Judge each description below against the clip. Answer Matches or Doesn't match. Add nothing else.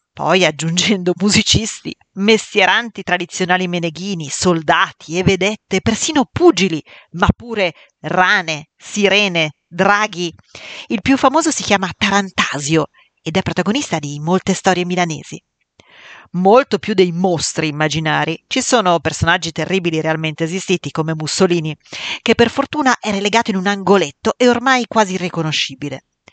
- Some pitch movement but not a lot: Matches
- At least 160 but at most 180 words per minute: Doesn't match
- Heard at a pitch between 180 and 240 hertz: Matches